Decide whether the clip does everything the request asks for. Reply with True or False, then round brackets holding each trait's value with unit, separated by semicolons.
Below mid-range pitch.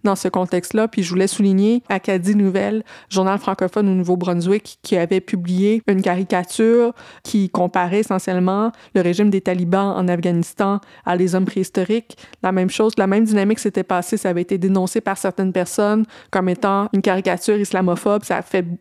False (195 Hz)